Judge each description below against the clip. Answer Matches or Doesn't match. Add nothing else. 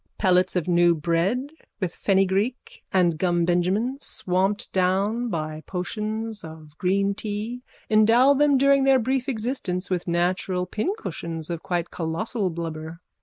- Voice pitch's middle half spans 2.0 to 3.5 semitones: Doesn't match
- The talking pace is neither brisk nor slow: Doesn't match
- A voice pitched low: Doesn't match